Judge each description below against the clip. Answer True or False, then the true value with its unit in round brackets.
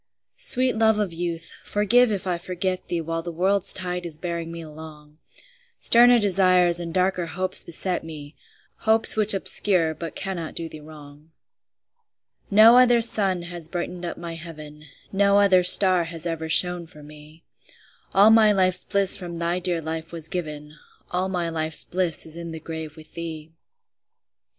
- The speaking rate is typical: True (165 wpm)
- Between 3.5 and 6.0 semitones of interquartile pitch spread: False (2.9 semitones)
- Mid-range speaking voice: True (175 Hz)